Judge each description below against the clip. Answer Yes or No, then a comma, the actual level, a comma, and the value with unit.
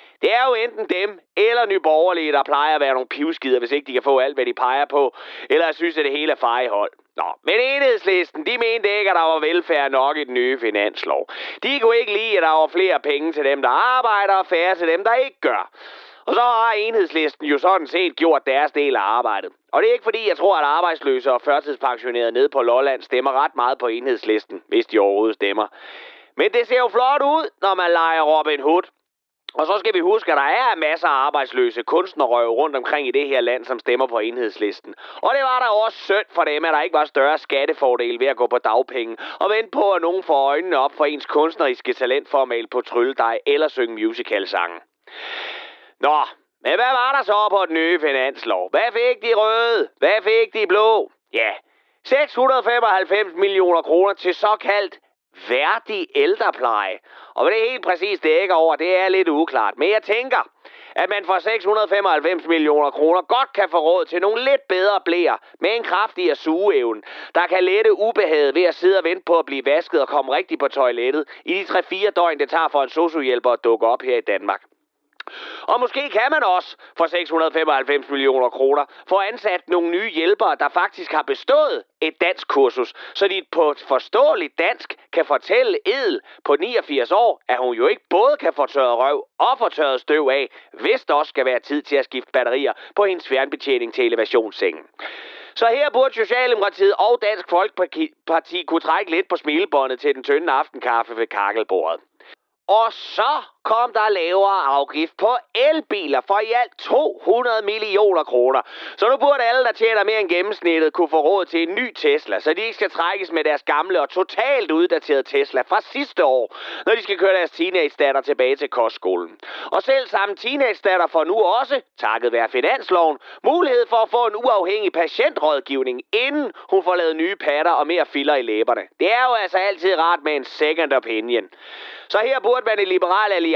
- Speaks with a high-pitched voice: Yes, high, 220 Hz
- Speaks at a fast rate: No, average, 200 wpm